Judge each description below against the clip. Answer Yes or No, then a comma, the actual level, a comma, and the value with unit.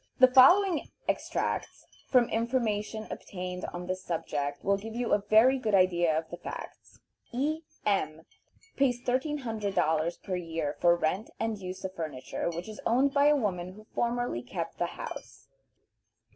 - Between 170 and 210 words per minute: No, average, 150 wpm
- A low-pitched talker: No, high, 200 Hz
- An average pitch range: No, wide, 5.9 semitones